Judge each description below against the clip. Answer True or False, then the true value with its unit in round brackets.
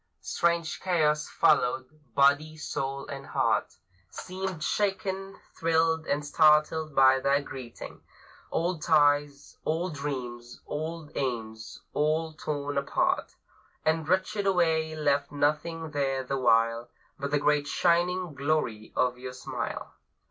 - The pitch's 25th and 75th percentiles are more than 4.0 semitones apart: False (3.0 semitones)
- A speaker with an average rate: False (120 wpm)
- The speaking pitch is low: False (150 Hz)